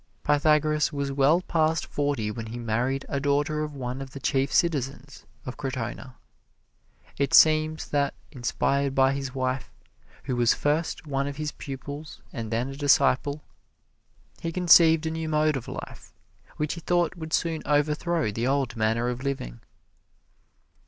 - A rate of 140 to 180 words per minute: Yes, average, 155 wpm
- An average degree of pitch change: Yes, average, 3.0 semitones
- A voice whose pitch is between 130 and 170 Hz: Yes, medium, 140 Hz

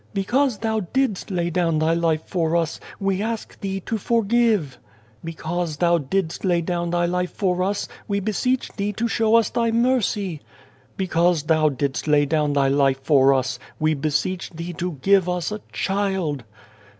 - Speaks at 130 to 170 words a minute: No, average, 180 wpm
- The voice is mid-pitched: Yes, medium, 175 Hz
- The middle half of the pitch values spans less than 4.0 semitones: No, average, 4.5 semitones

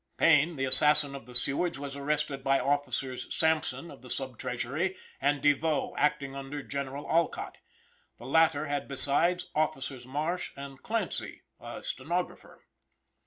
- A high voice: No, medium, 145 Hz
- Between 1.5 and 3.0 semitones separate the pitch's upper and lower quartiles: Yes, narrow, 2.5 semitones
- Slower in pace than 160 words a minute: Yes, average, 140 wpm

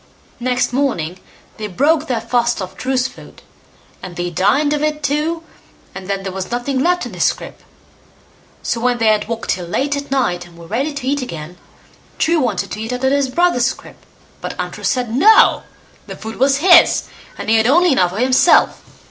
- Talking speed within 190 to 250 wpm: Yes, average, 200 wpm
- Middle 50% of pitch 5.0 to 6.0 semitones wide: Yes, wide, 5.4 semitones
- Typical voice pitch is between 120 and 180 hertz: No, very high, 250 Hz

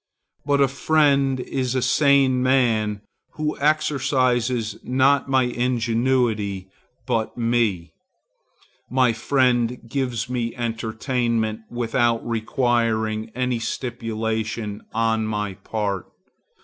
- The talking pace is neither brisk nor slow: No, slow, 95 wpm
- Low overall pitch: Yes, low, 120 Hz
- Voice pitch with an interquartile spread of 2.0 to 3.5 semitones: Yes, average, 2.7 semitones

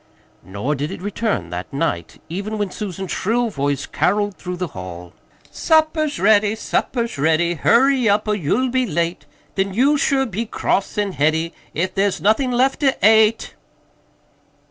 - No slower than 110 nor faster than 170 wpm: Yes, average, 155 wpm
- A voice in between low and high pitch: No, high, 200 Hz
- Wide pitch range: Yes, wide, 6.4 semitones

